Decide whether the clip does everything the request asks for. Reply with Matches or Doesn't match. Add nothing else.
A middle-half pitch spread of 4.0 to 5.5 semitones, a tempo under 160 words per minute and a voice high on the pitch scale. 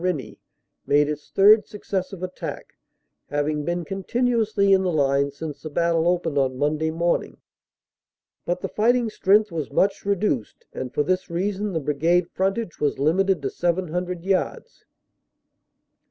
Doesn't match